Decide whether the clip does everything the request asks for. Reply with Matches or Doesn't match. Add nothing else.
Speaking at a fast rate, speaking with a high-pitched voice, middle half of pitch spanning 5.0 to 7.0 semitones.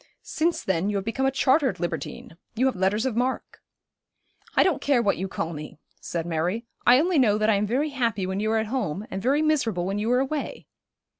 Matches